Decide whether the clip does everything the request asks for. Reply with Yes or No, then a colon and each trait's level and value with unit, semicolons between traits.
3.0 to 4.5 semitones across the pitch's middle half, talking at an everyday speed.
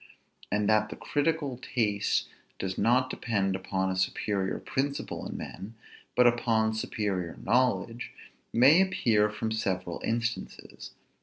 No: average, 3.7 semitones; slow, 125 wpm